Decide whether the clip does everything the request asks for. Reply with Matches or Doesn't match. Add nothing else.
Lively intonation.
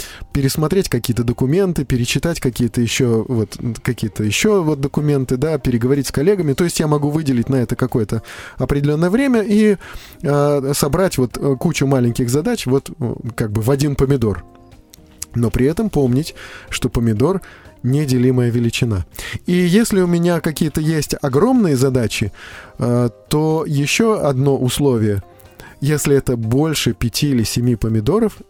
Doesn't match